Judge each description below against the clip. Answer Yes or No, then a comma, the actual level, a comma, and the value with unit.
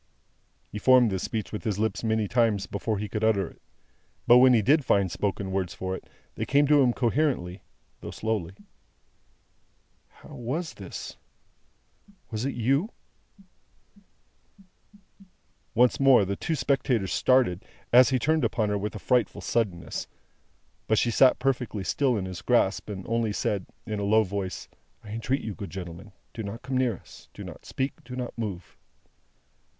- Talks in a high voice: No, low, 110 Hz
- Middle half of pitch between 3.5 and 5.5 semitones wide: Yes, average, 4.2 semitones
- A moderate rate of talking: Yes, average, 165 wpm